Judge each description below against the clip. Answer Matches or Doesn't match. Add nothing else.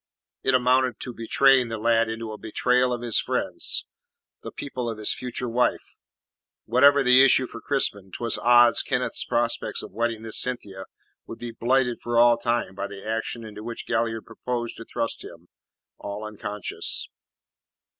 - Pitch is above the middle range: Doesn't match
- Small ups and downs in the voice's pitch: Matches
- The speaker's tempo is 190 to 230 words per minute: Doesn't match